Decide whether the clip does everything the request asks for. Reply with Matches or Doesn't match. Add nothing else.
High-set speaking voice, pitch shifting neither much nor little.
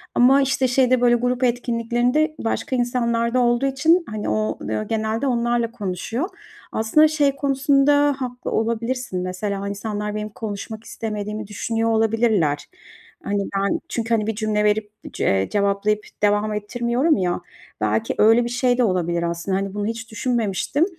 Matches